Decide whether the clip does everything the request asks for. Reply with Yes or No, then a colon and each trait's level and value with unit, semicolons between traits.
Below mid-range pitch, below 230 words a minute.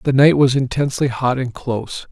Yes: low, 130 Hz; average, 200 wpm